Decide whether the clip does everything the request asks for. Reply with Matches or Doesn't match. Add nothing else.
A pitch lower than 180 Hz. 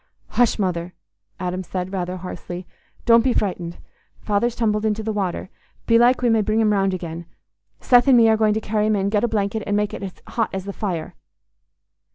Doesn't match